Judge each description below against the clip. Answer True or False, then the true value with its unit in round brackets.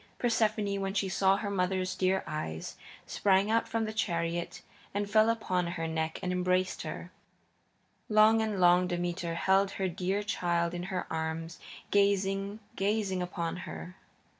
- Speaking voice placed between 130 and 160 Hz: False (190 Hz)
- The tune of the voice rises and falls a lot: False (2.7 semitones)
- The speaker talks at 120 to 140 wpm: False (150 wpm)